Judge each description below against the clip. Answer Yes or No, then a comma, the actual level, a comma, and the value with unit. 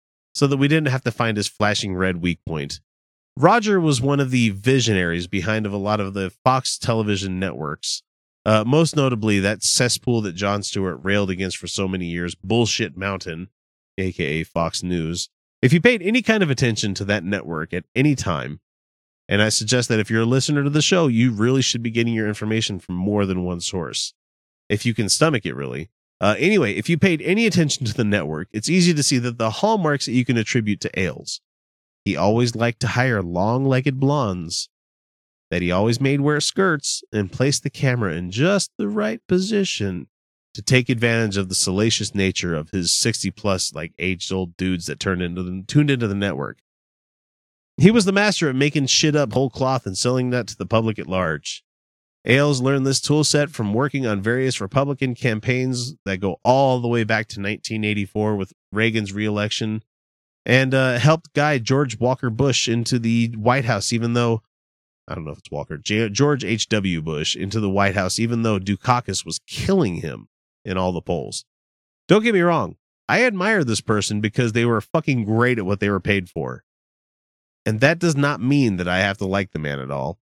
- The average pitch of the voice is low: Yes, low, 110 Hz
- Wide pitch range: Yes, wide, 5.9 semitones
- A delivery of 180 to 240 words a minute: Yes, average, 200 wpm